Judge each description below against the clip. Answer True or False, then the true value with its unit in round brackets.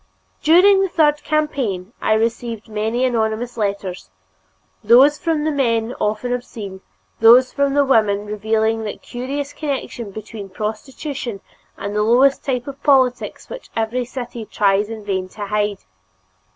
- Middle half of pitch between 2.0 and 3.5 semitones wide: False (4.5 semitones)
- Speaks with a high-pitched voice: True (230 Hz)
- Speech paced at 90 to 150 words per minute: True (140 wpm)